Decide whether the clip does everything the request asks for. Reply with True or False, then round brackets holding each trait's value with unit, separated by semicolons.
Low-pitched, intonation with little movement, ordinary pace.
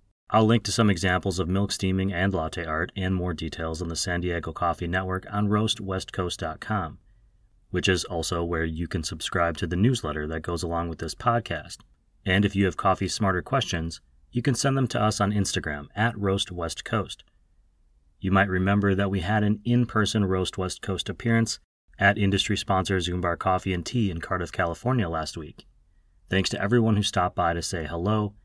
False (95 Hz; 3.4 semitones; 185 wpm)